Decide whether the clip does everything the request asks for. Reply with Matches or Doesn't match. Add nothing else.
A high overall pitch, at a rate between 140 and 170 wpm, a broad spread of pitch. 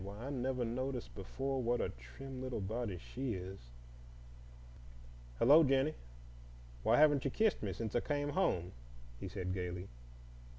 Doesn't match